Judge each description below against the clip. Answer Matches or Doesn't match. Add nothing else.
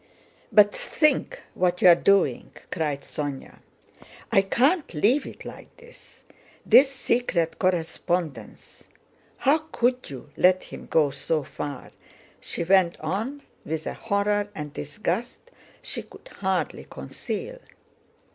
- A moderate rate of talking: Doesn't match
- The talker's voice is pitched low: Doesn't match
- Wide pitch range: Matches